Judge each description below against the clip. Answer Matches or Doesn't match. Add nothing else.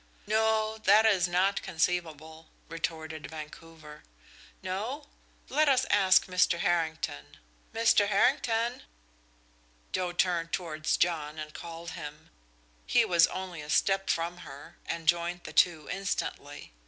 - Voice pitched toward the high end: Doesn't match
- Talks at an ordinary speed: Doesn't match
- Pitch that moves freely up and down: Doesn't match